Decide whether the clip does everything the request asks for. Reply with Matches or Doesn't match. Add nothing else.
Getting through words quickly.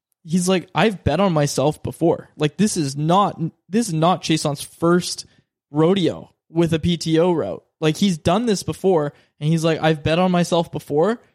Doesn't match